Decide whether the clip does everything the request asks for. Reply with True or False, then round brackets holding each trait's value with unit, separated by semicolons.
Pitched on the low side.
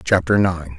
True (85 Hz)